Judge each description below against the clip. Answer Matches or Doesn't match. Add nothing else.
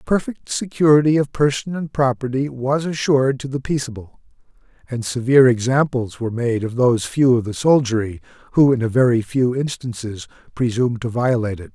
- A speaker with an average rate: Matches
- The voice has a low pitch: Matches